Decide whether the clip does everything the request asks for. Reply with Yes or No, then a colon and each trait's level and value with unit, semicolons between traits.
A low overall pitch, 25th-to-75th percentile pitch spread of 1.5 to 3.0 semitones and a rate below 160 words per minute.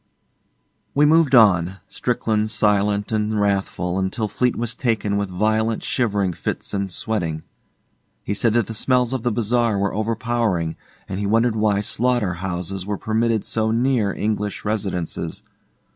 Yes: low, 105 Hz; average, 2.7 semitones; average, 145 wpm